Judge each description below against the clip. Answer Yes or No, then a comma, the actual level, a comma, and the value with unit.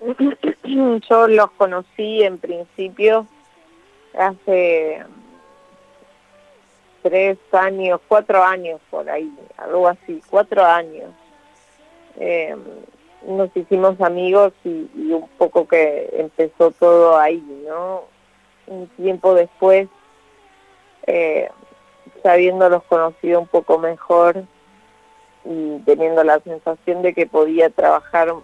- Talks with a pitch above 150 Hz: Yes, medium, 185 Hz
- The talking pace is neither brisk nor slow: No, slow, 100 wpm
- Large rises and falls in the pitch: No, average, 4.2 semitones